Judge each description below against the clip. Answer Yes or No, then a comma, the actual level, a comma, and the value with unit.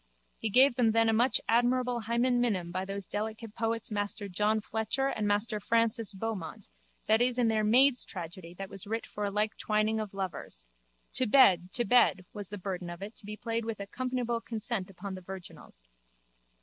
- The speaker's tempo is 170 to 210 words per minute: Yes, average, 190 wpm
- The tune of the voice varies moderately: Yes, average, 3.0 semitones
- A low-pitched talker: No, high, 215 Hz